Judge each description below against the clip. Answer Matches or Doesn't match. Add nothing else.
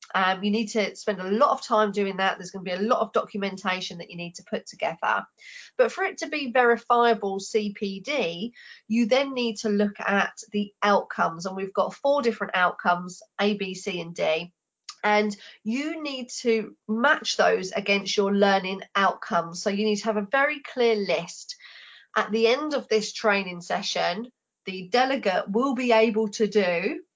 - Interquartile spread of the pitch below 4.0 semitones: Matches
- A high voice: Matches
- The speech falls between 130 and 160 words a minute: Doesn't match